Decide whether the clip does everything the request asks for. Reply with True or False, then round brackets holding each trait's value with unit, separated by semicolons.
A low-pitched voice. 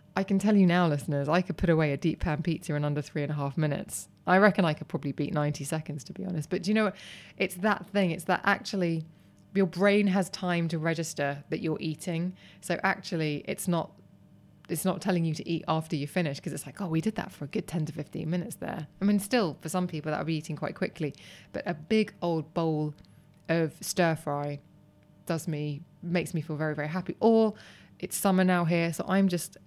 False (170 Hz)